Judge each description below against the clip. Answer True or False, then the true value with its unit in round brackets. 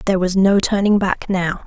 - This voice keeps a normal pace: False (215 wpm)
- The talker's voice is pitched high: True (195 Hz)